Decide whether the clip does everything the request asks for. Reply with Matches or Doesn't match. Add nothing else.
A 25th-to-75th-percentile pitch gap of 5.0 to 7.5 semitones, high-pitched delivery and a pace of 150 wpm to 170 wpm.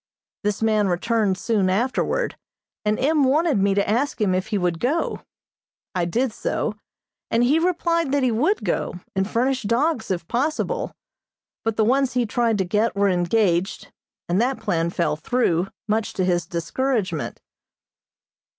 Matches